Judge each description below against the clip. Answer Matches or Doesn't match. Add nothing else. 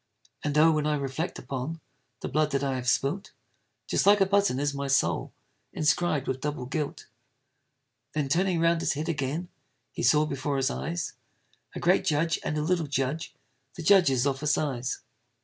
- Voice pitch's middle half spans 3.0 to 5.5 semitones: Matches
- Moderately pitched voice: Matches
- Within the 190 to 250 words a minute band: Doesn't match